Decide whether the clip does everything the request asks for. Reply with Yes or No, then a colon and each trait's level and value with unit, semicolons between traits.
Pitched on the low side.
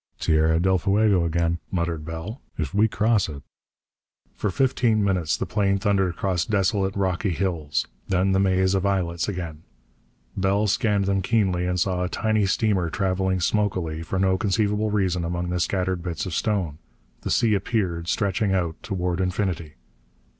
Yes: very low, 95 Hz